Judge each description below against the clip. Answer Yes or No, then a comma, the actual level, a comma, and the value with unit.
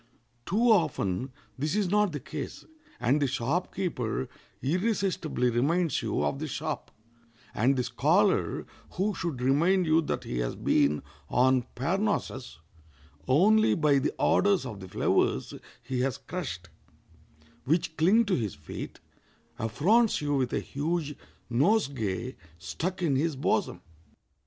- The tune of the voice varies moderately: No, wide, 6.5 semitones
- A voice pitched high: No, medium, 150 Hz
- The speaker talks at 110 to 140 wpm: Yes, slow, 135 wpm